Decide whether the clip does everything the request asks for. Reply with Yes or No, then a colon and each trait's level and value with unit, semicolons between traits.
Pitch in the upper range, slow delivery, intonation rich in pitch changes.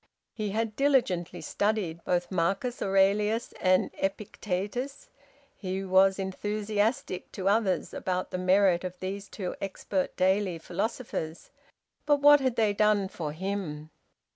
No: high, 195 Hz; slow, 125 wpm; narrow, 2.6 semitones